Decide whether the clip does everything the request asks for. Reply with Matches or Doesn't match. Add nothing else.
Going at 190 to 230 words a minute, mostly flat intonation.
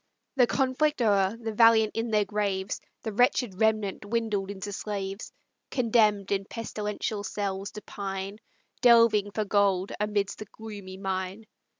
Doesn't match